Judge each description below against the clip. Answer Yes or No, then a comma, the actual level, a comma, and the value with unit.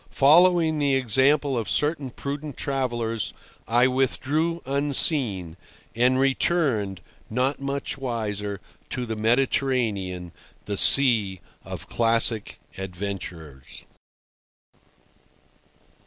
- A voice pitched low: Yes, low, 125 Hz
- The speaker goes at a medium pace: No, slow, 80 wpm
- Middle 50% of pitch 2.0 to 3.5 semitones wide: No, average, 5.1 semitones